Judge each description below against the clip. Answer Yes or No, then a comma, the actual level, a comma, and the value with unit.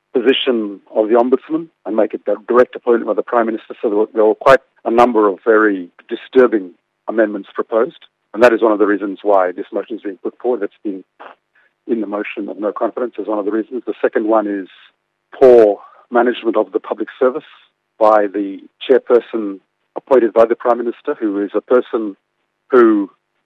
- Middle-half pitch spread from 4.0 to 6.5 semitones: No, average, 2.8 semitones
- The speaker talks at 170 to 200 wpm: Yes, average, 190 wpm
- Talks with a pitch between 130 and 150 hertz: No, low, 110 Hz